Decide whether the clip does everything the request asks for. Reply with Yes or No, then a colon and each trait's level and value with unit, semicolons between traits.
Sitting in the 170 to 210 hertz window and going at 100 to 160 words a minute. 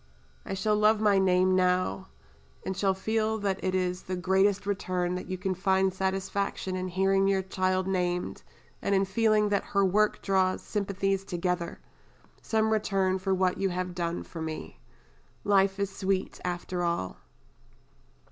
Yes: high, 190 Hz; average, 155 wpm